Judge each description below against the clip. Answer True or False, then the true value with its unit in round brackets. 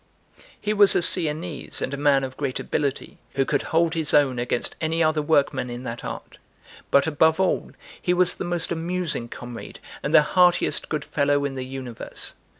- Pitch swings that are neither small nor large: True (3.7 semitones)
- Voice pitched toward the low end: False (150 Hz)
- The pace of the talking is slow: False (185 wpm)